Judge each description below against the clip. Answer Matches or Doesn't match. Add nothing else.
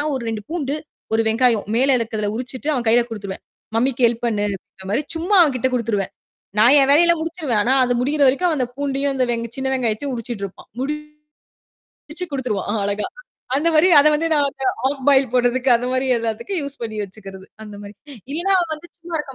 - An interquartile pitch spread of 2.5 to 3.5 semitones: Doesn't match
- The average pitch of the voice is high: Matches